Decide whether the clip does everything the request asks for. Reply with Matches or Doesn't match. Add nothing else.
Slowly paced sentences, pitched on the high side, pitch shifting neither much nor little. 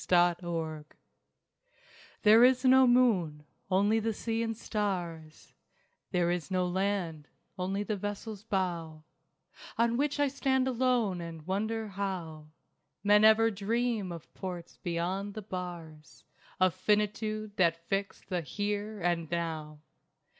Matches